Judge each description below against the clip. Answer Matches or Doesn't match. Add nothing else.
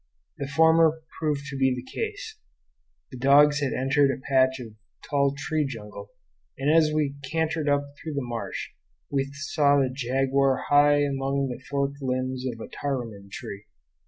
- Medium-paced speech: Matches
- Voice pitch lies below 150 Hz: Matches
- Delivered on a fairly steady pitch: Matches